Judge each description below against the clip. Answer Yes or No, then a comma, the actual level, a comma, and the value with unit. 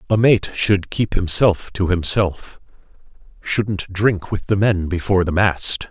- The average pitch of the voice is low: Yes, very low, 95 Hz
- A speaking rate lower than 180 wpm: Yes, average, 140 wpm